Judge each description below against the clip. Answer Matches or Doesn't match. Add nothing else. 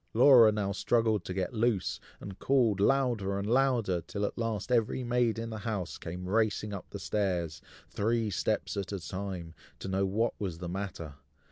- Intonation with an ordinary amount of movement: Matches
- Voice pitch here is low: Matches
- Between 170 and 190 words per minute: Matches